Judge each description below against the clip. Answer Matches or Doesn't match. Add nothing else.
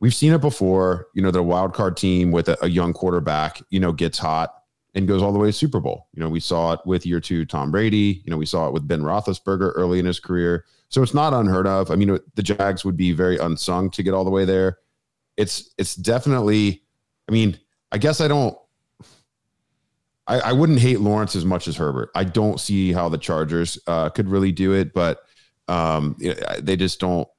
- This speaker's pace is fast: Matches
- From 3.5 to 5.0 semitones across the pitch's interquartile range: Doesn't match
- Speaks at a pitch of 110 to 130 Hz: Doesn't match